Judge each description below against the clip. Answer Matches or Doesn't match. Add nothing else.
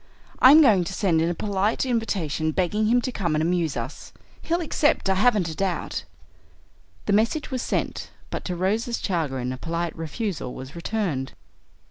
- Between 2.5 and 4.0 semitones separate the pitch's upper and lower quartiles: Doesn't match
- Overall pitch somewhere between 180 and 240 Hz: Matches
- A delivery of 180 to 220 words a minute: Doesn't match